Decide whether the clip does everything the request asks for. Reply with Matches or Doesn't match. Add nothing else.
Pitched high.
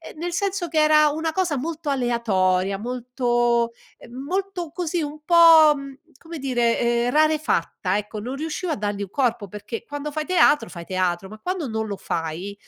Matches